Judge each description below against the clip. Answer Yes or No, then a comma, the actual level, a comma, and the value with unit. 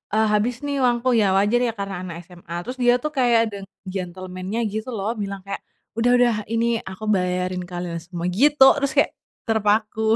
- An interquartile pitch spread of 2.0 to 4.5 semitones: Yes, average, 4.2 semitones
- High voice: Yes, high, 215 Hz